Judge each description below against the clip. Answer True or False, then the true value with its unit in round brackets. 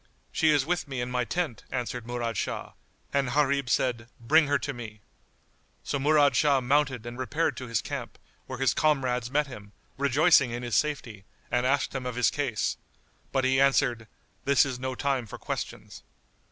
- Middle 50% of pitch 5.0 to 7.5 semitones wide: False (2.7 semitones)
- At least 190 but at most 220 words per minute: False (180 wpm)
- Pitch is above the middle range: False (130 Hz)